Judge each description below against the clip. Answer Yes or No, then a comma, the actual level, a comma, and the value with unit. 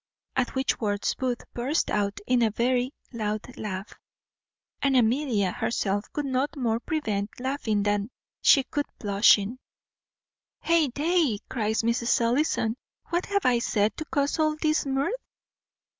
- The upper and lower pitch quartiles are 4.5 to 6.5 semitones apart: Yes, average, 4.8 semitones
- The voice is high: Yes, high, 245 Hz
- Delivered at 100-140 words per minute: Yes, slow, 135 wpm